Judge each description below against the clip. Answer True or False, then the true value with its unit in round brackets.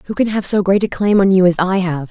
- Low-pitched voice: False (190 Hz)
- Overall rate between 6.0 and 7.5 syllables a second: True (6.2 syllables/s)